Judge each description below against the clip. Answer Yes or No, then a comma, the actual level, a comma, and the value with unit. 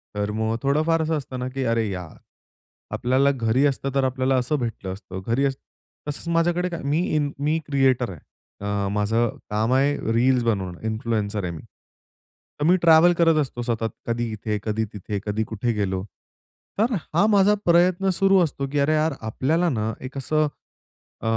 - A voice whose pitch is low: Yes, low, 130 Hz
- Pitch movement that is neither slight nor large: No, wide, 5.8 semitones